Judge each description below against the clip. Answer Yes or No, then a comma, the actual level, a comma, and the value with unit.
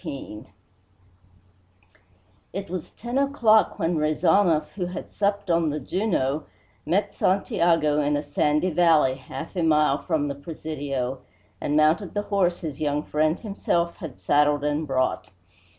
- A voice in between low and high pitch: Yes, medium, 160 Hz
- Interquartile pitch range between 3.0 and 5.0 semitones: Yes, average, 3.8 semitones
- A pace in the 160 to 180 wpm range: No, average, 140 wpm